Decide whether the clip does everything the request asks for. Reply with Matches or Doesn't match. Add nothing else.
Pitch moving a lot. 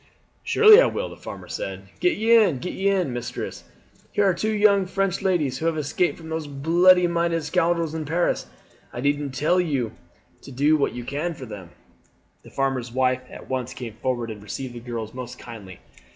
Matches